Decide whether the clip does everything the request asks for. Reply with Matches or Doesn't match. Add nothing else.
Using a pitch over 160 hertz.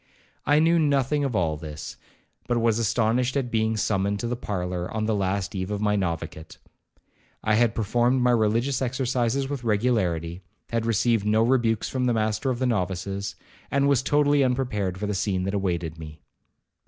Doesn't match